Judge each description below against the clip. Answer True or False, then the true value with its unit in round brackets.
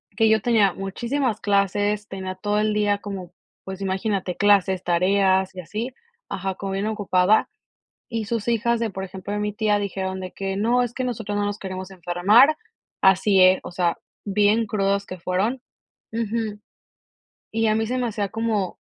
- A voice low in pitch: False (205 Hz)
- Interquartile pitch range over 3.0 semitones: False (2.4 semitones)